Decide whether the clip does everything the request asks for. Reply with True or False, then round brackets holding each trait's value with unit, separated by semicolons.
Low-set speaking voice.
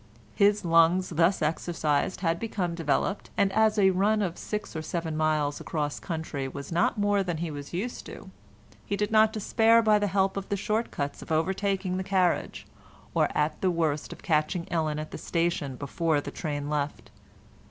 False (175 Hz)